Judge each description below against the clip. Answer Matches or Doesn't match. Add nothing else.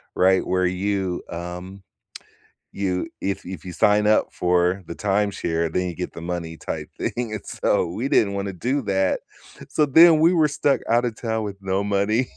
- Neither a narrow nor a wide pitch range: Matches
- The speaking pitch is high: Doesn't match